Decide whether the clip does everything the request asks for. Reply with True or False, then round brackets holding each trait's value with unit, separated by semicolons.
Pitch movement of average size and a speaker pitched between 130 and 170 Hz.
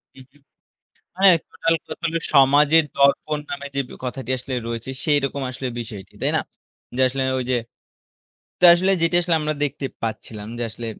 True (3.4 semitones; 140 Hz)